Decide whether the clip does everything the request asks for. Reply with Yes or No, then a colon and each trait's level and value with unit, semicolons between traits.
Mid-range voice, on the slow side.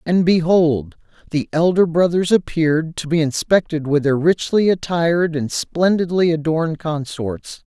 Yes: medium, 160 Hz; slow, 130 wpm